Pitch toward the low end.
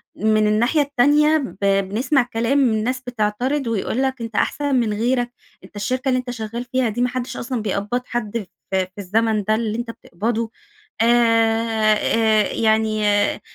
No: high, 230 Hz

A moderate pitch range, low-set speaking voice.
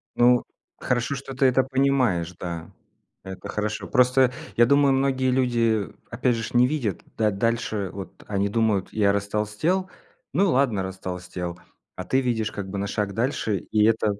Yes: average, 4.4 semitones; low, 115 Hz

